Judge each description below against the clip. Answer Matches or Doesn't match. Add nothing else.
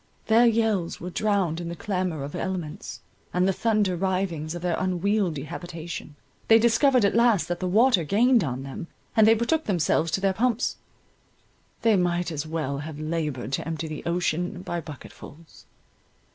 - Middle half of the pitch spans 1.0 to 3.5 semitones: Doesn't match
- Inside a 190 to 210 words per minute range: Doesn't match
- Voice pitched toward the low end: Doesn't match